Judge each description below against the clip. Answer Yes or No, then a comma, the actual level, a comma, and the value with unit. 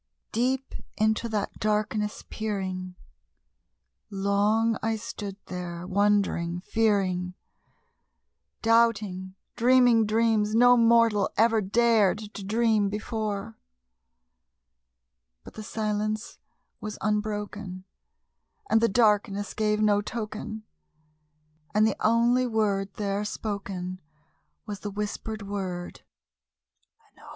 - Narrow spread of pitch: Yes, narrow, 2.0 semitones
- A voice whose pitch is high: Yes, high, 210 Hz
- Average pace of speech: No, slow, 95 wpm